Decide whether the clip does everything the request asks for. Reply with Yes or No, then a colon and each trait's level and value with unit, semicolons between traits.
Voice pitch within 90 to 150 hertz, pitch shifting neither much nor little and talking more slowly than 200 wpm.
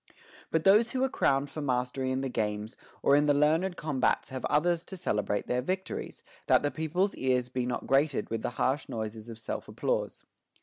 No: low, 135 Hz; average, 4.4 semitones; fast, 205 wpm